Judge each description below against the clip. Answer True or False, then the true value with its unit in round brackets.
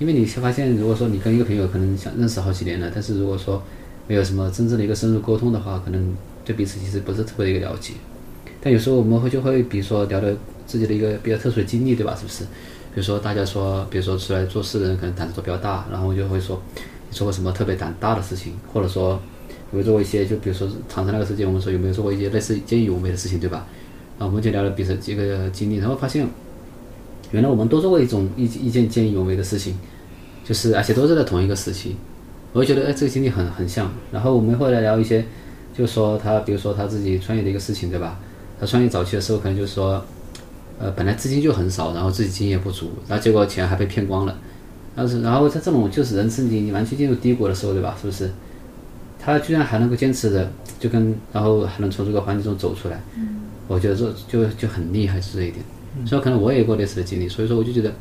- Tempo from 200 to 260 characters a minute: False (395 characters per minute)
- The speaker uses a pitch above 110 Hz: False (105 Hz)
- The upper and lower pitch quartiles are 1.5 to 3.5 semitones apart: True (3.2 semitones)